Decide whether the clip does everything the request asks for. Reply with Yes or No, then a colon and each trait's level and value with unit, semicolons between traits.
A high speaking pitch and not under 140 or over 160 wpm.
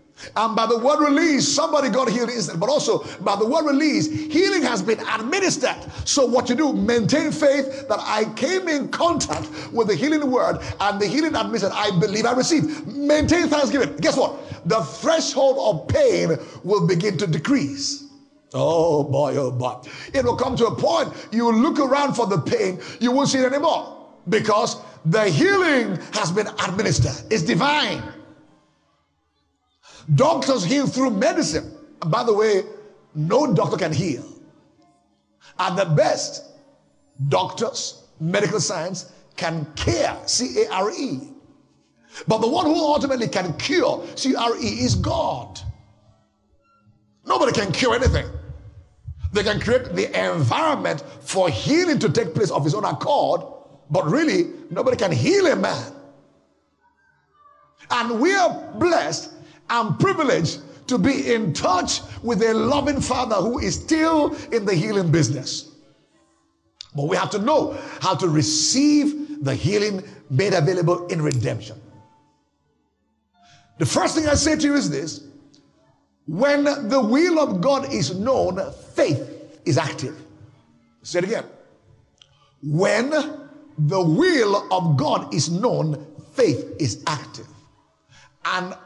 Yes: high, 225 Hz; average, 145 wpm